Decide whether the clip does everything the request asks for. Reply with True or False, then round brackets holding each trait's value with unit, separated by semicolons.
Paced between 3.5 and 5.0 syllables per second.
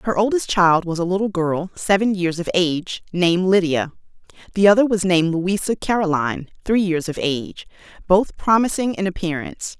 False (5.4 syllables/s)